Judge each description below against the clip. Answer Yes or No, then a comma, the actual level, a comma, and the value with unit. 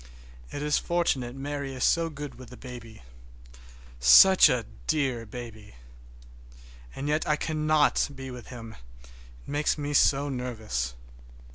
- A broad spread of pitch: No, average, 3.8 semitones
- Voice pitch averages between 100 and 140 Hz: Yes, low, 135 Hz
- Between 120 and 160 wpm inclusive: Yes, slow, 135 wpm